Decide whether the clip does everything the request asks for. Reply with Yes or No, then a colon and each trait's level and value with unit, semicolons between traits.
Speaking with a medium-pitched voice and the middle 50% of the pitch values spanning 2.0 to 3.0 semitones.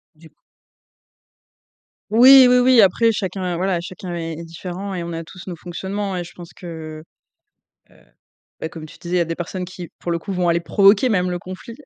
Yes: medium, 180 Hz; narrow, 2.6 semitones